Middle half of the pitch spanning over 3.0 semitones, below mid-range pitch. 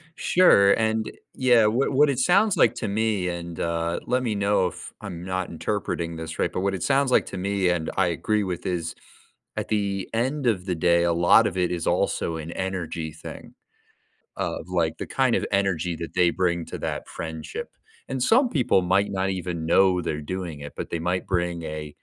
Yes: average, 4.0 semitones; very low, 90 Hz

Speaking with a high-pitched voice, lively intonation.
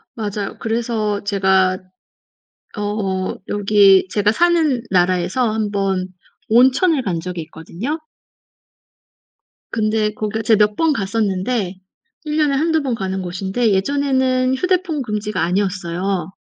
No: high, 210 Hz; average, 4.9 semitones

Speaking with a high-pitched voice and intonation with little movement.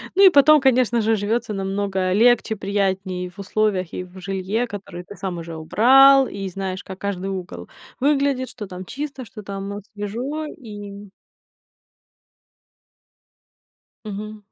No: high, 205 Hz; average, 4.0 semitones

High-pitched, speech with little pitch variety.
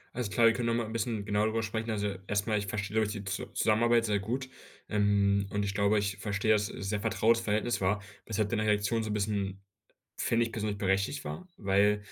No: low, 105 Hz; narrow, 1.8 semitones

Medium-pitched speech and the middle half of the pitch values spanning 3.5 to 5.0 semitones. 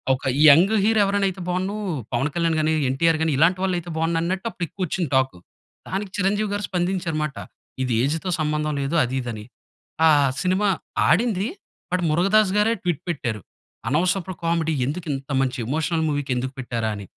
Yes: medium, 165 Hz; average, 4.5 semitones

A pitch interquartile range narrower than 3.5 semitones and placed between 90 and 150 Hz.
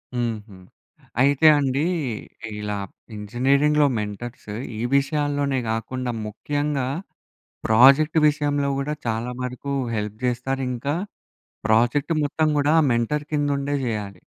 No: average, 3.9 semitones; low, 135 Hz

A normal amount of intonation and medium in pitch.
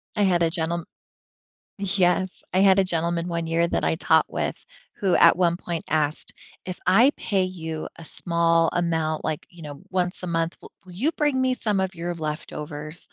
No: narrow, 2.3 semitones; medium, 170 Hz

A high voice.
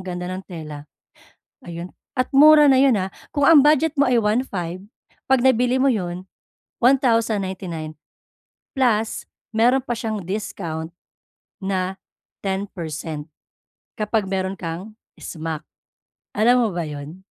Yes: high, 195 Hz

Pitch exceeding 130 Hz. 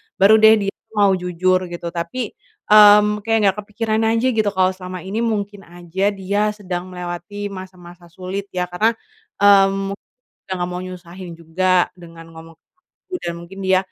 Yes: high, 190 Hz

